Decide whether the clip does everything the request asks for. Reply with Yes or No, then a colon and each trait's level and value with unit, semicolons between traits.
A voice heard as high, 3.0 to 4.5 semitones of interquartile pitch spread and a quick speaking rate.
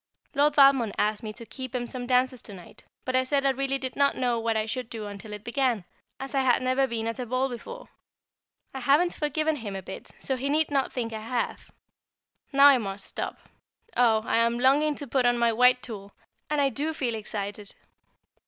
Yes: very high, 250 Hz; average, 3.3 semitones; fast, 220 wpm